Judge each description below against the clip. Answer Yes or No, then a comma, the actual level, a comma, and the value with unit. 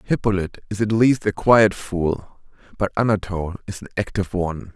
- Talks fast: No, average, 165 wpm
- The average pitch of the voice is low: Yes, low, 100 Hz